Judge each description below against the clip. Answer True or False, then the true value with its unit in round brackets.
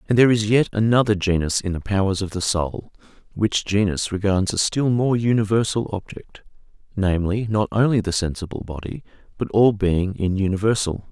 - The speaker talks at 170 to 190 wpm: False (160 wpm)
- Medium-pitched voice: False (100 Hz)